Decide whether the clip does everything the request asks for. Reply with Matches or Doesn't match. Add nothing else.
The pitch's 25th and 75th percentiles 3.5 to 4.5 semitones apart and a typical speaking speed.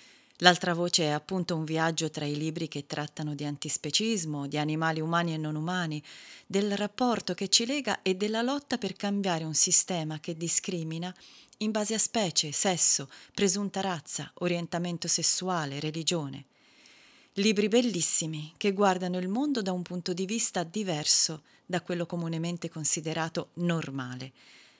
Matches